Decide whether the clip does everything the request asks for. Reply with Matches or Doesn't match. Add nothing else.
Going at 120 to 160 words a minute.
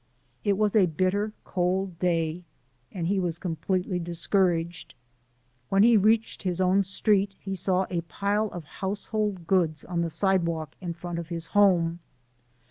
Matches